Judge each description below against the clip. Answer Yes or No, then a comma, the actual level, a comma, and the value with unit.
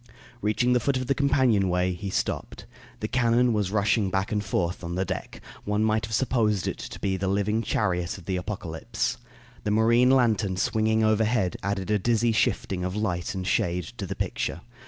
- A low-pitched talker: Yes, low, 105 Hz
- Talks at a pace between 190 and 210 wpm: Yes, average, 195 wpm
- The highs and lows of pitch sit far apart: No, average, 3.2 semitones